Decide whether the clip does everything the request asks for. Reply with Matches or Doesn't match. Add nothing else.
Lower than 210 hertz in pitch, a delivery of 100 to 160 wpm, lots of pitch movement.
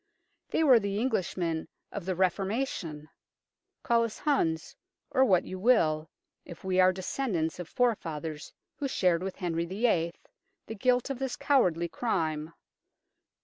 Matches